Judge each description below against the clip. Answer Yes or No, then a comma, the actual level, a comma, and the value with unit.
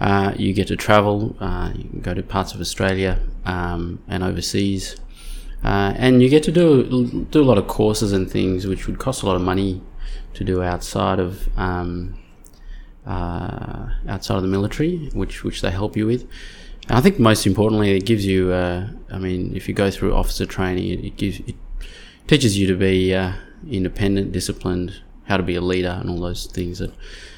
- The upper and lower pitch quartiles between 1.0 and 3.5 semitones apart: Yes, narrow, 2.6 semitones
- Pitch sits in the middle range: No, very low, 95 Hz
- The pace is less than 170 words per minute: No, average, 195 wpm